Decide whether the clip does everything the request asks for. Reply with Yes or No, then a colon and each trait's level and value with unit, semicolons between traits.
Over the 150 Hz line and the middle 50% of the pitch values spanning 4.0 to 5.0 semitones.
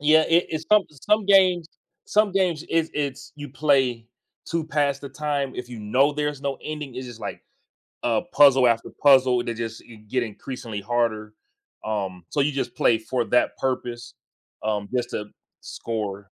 No: low, 130 Hz; average, 4.5 semitones